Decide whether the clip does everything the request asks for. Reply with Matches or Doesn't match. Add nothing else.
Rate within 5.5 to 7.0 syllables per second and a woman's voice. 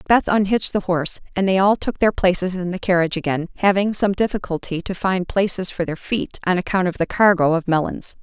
Matches